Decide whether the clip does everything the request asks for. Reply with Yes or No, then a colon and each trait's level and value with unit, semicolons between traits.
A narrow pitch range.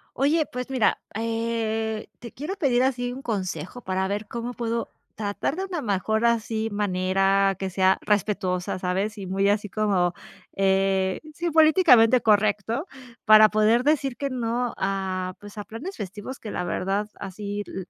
No: average, 3.8 semitones